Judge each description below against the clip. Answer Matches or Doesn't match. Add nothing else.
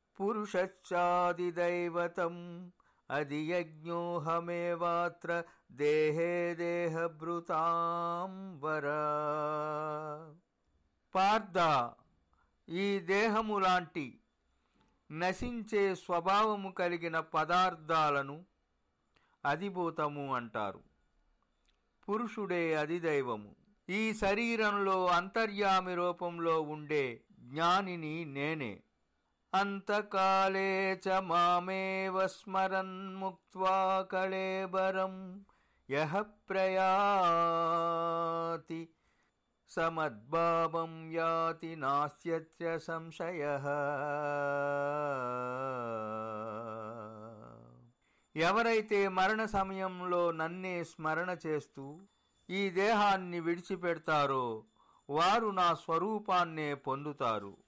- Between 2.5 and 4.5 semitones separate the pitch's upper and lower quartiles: Matches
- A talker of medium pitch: Matches